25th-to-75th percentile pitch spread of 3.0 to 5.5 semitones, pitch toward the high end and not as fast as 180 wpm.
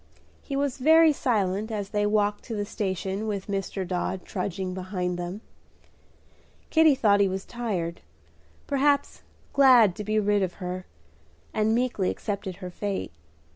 Yes: average, 3.5 semitones; high, 205 Hz; average, 145 wpm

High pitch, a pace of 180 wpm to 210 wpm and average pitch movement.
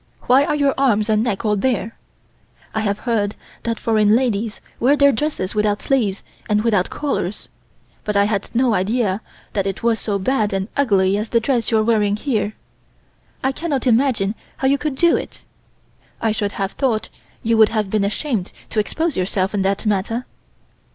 Yes: high, 220 Hz; average, 185 wpm; average, 3.8 semitones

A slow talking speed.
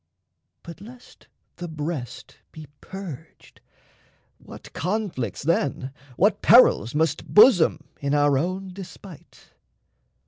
Yes: slow, 100 wpm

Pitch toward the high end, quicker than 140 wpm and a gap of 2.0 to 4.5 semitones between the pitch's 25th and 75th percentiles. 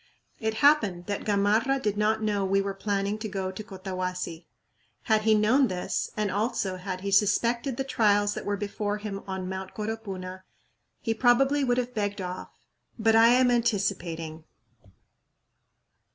Yes: high, 205 Hz; average, 155 wpm; average, 2.8 semitones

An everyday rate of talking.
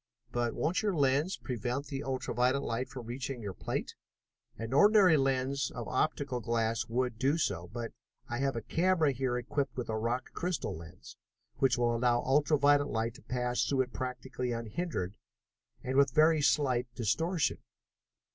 Yes: average, 170 wpm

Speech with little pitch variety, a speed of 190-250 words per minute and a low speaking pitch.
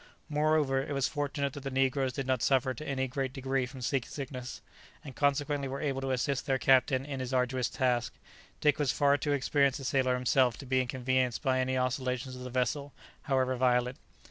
Yes: narrow, 1.5 semitones; average, 200 wpm; low, 130 Hz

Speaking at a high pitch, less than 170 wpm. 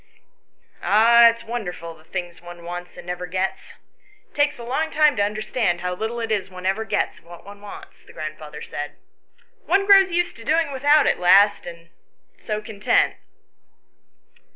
No: high, 210 Hz; average, 175 wpm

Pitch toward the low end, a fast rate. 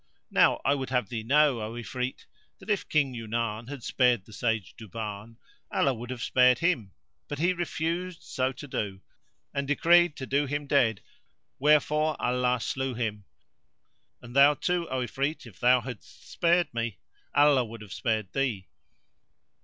No: low, 125 Hz; average, 160 wpm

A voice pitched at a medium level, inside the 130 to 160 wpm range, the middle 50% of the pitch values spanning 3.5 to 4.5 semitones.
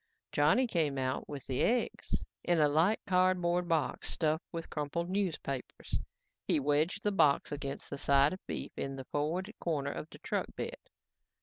No: medium, 155 Hz; average, 170 wpm; average, 4.0 semitones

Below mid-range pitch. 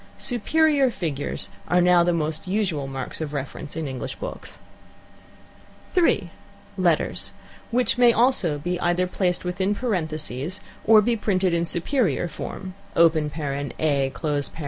No: medium, 175 Hz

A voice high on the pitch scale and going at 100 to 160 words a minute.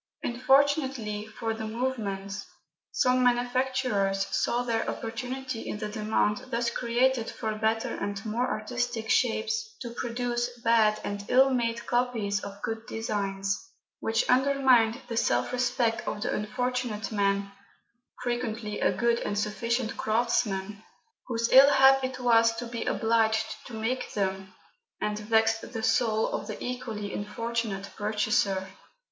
Yes: high, 230 Hz; slow, 135 wpm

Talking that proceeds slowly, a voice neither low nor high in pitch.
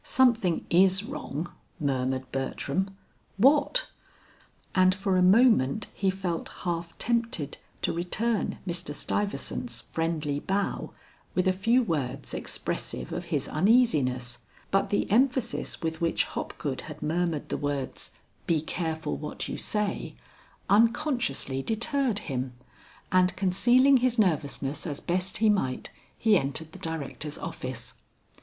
Yes: slow, 125 wpm; medium, 180 Hz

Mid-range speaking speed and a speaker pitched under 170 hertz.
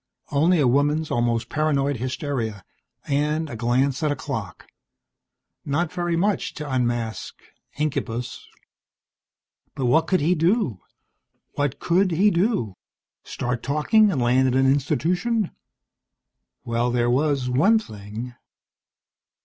No: slow, 120 wpm; medium, 140 Hz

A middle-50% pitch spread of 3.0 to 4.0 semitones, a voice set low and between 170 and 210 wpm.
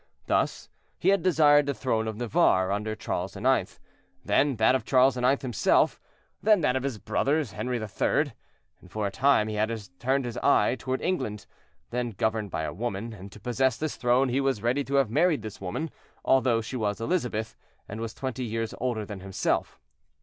Yes: average, 3.7 semitones; low, 120 Hz; average, 185 wpm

